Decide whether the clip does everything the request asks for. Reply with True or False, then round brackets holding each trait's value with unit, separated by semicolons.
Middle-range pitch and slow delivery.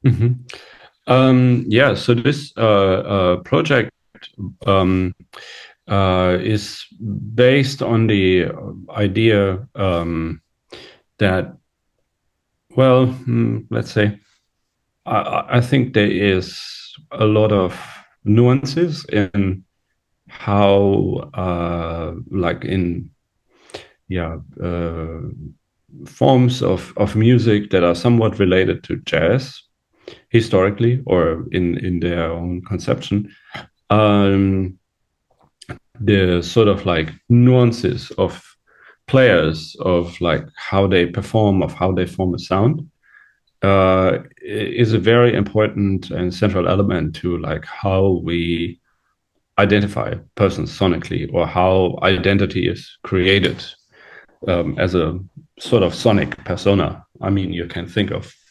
False (100 Hz; 110 wpm)